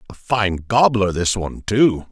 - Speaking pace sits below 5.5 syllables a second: Yes, 4.3 syllables/s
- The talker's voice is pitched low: Yes, low, 105 Hz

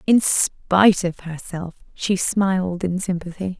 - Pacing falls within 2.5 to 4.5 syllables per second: Yes, 4.0 syllables/s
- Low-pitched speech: No, medium, 180 Hz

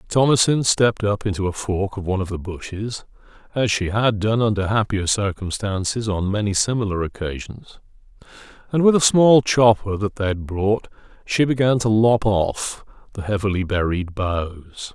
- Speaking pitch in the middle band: No, low, 105 Hz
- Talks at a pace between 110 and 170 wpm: Yes, average, 160 wpm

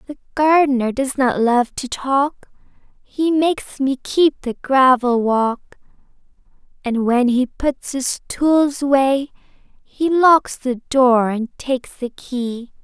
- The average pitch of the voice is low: No, very high, 265 Hz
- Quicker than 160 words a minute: No, slow, 135 wpm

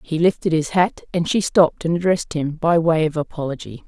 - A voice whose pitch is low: No, medium, 160 Hz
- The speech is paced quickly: Yes, fast, 215 wpm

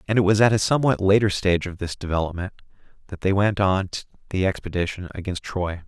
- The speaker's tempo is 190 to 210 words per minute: Yes, average, 195 wpm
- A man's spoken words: Yes, male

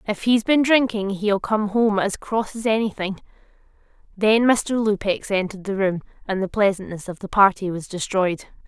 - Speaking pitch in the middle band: No, high, 205 Hz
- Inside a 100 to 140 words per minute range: No, average, 175 wpm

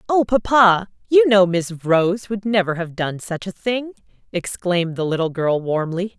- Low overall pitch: No, high, 190 Hz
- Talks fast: No, average, 175 wpm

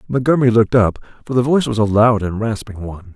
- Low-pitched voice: Yes, low, 110 Hz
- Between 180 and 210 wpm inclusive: No, fast, 230 wpm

